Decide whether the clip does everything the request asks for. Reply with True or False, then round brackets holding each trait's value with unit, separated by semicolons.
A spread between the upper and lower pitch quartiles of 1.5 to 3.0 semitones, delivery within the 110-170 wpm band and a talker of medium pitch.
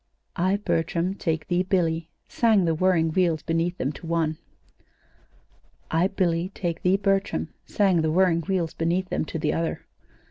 True (2.4 semitones; 155 wpm; 170 Hz)